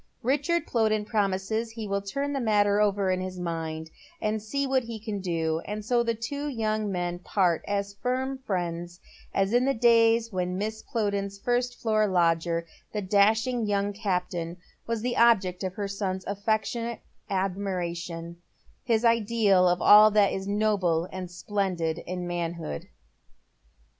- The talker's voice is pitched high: Yes, high, 200 Hz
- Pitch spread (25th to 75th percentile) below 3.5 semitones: No, average, 3.8 semitones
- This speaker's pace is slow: No, average, 160 wpm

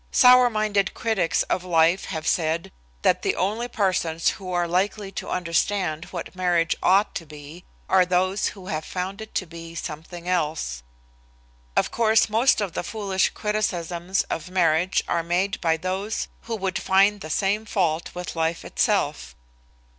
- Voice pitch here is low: No, medium, 185 Hz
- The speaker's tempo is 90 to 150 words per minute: No, average, 160 wpm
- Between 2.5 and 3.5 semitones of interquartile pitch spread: Yes, average, 3.2 semitones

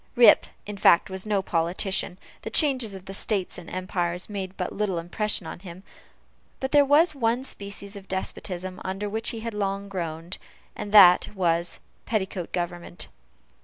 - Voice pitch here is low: No, high, 195 Hz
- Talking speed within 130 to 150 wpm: No, average, 160 wpm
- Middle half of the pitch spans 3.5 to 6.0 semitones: No, average, 2.9 semitones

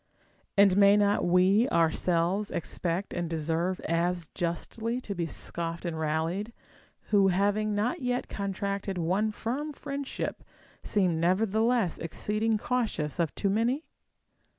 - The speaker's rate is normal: No, slow, 130 wpm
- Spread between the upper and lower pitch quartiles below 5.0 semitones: Yes, average, 4.2 semitones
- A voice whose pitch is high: Yes, high, 195 Hz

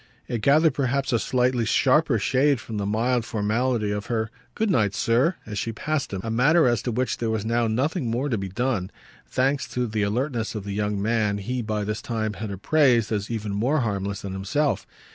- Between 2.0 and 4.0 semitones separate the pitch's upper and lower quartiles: Yes, average, 3.6 semitones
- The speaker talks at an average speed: No, fast, 210 wpm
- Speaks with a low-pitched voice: Yes, low, 115 Hz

